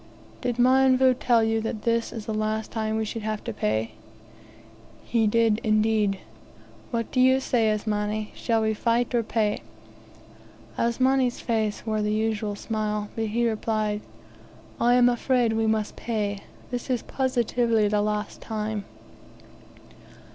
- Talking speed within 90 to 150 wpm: Yes, average, 145 wpm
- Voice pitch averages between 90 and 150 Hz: No, high, 220 Hz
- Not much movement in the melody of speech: Yes, narrow, 1.9 semitones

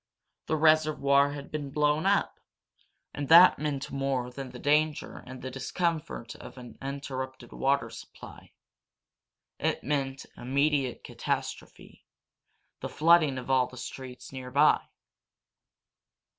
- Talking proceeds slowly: Yes, slow, 120 wpm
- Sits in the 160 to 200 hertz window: No, medium, 140 Hz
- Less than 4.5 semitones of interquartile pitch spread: Yes, narrow, 2.5 semitones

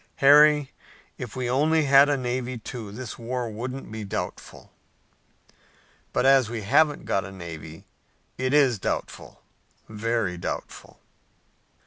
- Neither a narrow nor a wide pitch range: Yes, average, 4.1 semitones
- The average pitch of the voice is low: Yes, low, 125 Hz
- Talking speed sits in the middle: No, slow, 125 wpm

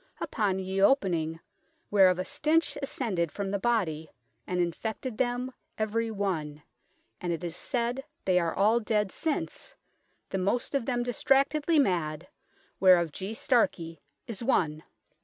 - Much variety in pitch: Yes, wide, 5.7 semitones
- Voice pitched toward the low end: No, high, 200 Hz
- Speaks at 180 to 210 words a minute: No, average, 140 wpm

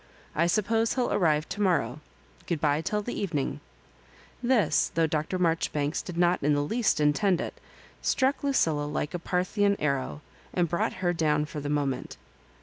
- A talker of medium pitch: Yes, medium, 165 Hz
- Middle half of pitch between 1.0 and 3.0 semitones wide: No, average, 5.0 semitones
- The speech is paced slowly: No, average, 165 wpm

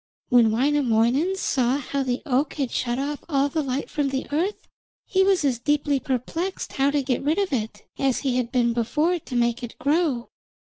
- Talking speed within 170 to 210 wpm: Yes, average, 195 wpm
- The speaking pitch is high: Yes, very high, 275 Hz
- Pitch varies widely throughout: No, average, 3.3 semitones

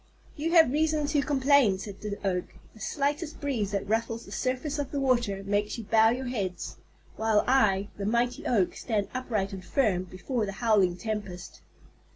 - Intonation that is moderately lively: Yes, average, 5.0 semitones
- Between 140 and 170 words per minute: No, average, 180 wpm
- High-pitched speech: Yes, high, 225 Hz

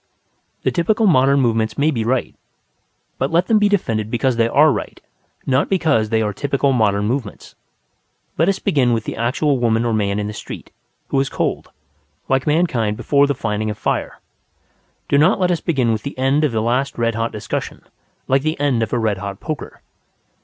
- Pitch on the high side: No, low, 130 Hz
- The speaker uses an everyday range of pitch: Yes, average, 4.4 semitones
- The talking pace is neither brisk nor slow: Yes, average, 195 wpm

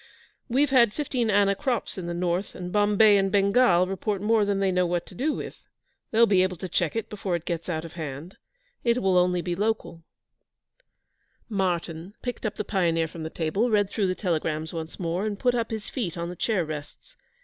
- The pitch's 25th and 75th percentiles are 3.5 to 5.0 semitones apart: Yes, average, 3.8 semitones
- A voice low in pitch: No, high, 190 Hz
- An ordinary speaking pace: No, fast, 210 wpm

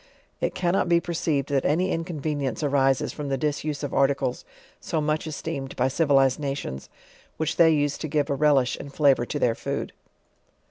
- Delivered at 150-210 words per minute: Yes, average, 175 wpm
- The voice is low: No, medium, 145 Hz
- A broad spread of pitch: No, narrow, 2.5 semitones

